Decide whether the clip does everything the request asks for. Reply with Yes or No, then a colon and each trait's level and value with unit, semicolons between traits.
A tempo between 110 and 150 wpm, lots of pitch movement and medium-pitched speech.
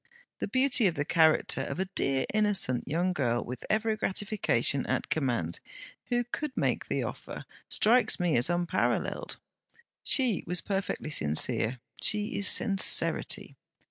Yes: average, 140 wpm; wide, 7.8 semitones; medium, 180 Hz